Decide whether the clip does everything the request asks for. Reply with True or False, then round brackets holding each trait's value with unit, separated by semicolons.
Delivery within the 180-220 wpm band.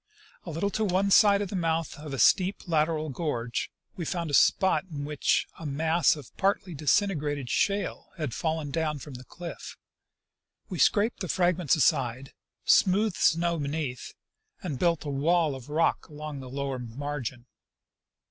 False (165 wpm)